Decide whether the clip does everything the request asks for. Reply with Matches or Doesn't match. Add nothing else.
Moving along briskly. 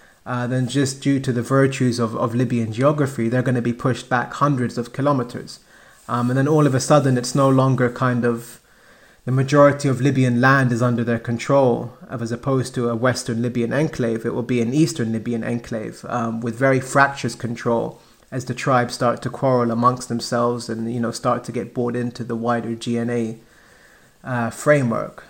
Doesn't match